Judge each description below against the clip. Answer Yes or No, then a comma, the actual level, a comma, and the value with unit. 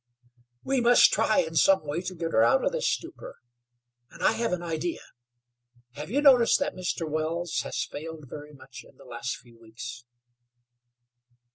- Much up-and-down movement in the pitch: Yes, wide, 7.7 semitones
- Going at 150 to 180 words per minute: Yes, average, 170 wpm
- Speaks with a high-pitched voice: No, medium, 165 Hz